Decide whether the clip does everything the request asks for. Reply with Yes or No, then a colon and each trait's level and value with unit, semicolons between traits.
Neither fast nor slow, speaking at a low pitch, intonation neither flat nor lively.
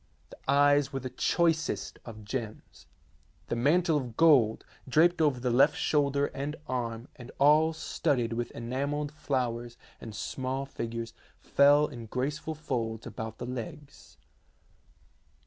No: slow, 130 wpm; low, 130 Hz; average, 3.9 semitones